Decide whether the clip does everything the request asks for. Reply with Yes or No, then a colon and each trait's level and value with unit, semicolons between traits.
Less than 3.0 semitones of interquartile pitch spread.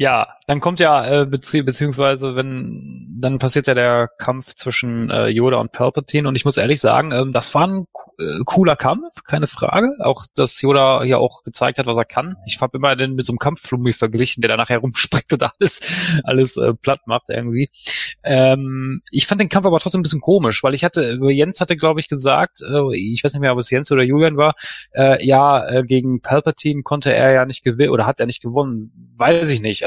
Yes: narrow, 2.6 semitones